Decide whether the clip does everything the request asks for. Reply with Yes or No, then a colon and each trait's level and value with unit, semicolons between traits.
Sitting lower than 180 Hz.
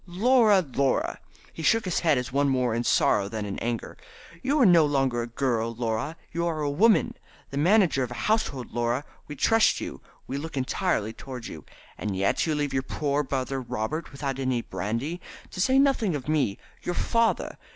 Yes: medium, 140 Hz